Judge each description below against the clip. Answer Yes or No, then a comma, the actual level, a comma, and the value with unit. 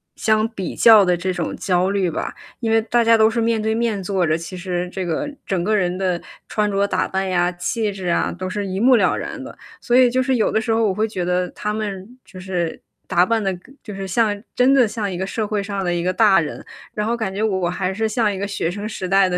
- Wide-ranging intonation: No, average, 3.2 semitones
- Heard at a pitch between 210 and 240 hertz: No, high, 200 Hz